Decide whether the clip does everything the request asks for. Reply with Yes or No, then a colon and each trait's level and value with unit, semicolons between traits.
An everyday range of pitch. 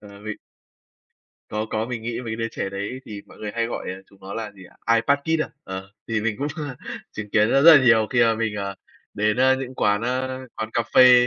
Yes: average, 3.1 semitones